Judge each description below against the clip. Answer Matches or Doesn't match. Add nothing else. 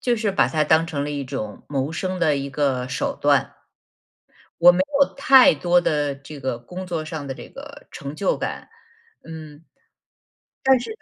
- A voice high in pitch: Doesn't match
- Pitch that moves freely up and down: Doesn't match